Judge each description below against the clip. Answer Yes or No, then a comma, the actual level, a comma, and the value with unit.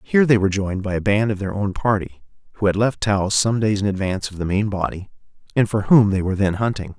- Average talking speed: No, fast, 260 wpm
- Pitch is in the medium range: No, low, 100 Hz